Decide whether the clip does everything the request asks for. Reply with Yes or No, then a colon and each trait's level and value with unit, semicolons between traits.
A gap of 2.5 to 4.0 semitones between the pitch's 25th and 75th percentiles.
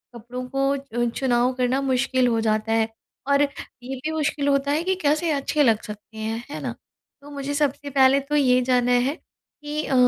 Yes: average, 2.8 semitones